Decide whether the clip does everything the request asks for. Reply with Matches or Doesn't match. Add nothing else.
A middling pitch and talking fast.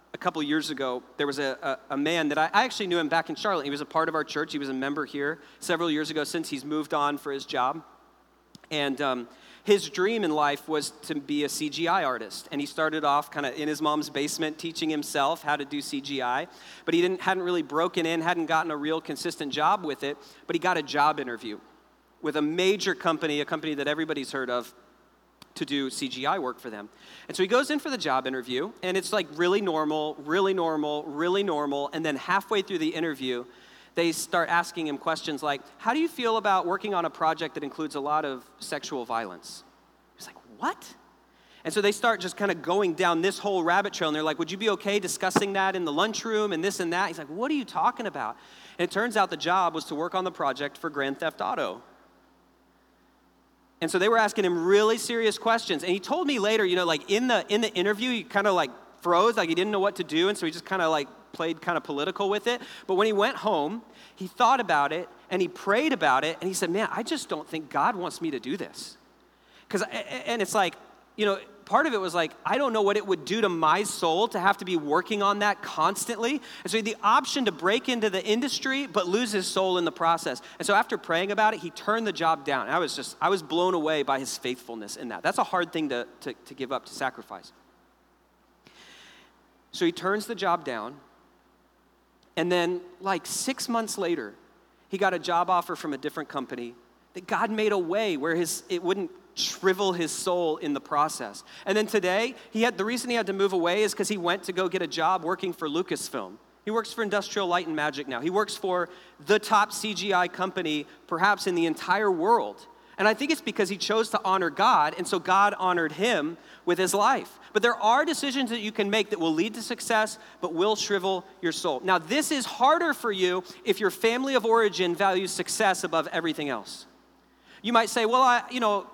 Matches